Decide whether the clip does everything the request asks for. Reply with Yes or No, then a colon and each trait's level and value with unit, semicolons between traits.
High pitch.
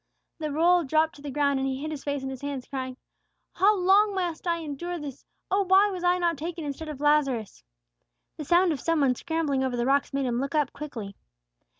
Yes: very high, 295 Hz